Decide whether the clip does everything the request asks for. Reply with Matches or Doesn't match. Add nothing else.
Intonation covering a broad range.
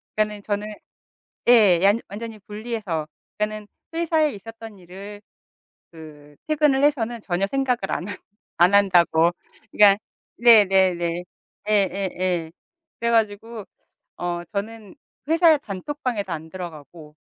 Doesn't match